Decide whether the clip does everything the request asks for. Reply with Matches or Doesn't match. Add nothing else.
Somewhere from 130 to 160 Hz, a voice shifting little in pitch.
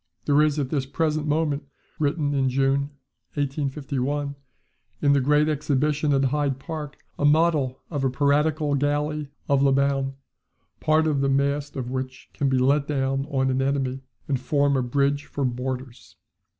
Matches